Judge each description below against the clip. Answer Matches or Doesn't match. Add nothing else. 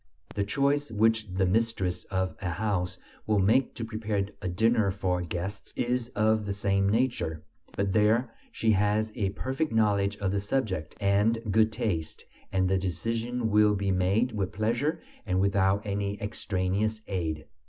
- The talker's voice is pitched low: Matches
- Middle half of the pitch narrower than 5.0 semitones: Matches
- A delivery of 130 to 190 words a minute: Matches